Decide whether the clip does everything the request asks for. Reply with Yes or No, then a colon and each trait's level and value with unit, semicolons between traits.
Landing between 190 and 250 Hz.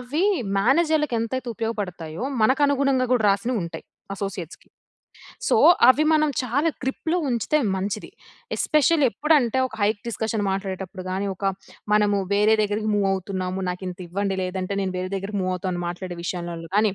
Yes: high, 205 Hz